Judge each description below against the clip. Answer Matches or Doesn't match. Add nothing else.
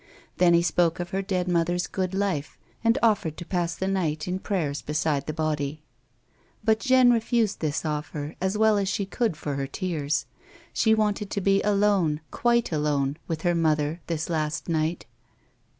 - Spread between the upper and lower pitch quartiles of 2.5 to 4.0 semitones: Doesn't match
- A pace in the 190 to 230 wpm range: Doesn't match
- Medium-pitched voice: Matches